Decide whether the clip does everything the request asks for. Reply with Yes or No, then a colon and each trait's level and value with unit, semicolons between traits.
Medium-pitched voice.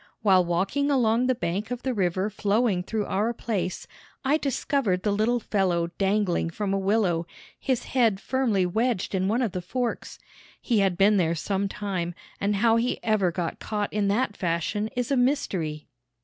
No: high, 205 Hz